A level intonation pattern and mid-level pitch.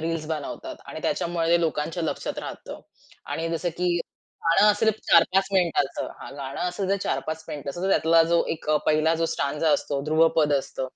Yes: narrow, 2.1 semitones; medium, 165 Hz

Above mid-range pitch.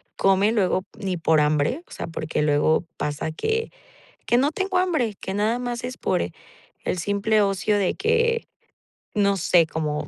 Yes: high, 200 Hz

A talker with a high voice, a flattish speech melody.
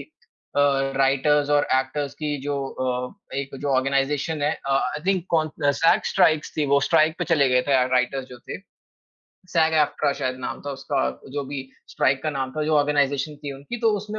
No: medium, 145 Hz; narrow, 2.2 semitones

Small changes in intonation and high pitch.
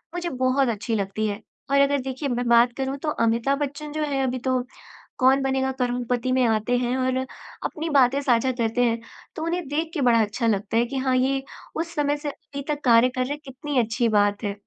No: average, 3.0 semitones; very high, 255 Hz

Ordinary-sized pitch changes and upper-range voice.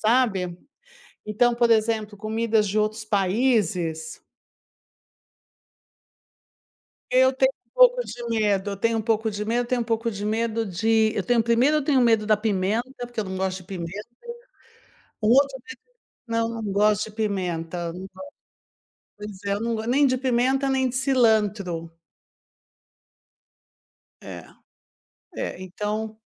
Yes: average, 3.1 semitones; high, 220 Hz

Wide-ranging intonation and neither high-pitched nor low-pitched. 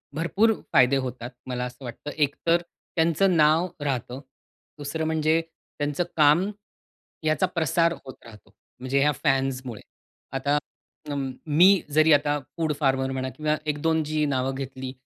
No: average, 3.3 semitones; medium, 145 Hz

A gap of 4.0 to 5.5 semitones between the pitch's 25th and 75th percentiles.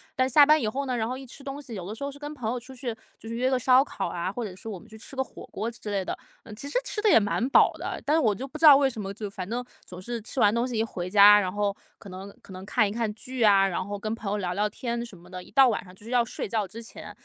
Yes: average, 4.3 semitones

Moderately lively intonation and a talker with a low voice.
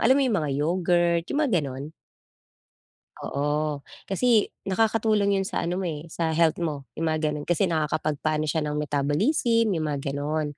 No: average, 4.4 semitones; medium, 160 Hz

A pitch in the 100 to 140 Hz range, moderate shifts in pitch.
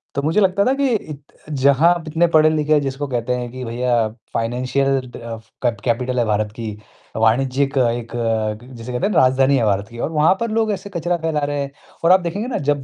Yes: low, 135 Hz; average, 5.0 semitones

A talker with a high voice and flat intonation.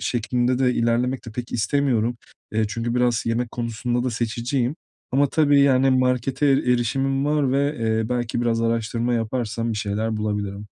No: low, 120 Hz; narrow, 2.1 semitones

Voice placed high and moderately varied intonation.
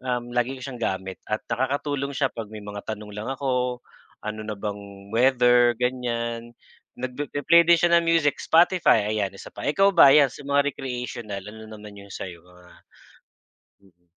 No: low, 120 Hz; average, 4.4 semitones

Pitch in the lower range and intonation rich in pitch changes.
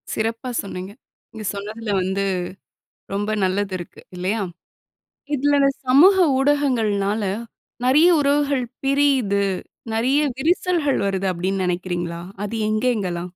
No: high, 220 Hz; wide, 6.0 semitones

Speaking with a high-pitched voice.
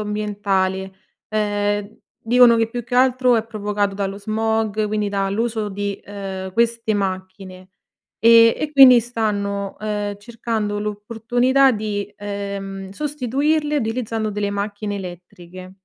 Yes: high, 210 Hz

